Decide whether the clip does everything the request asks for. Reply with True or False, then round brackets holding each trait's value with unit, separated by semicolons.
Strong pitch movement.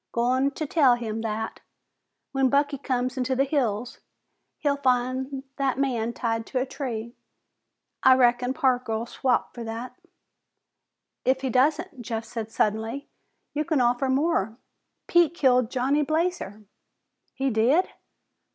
False (2.8 semitones)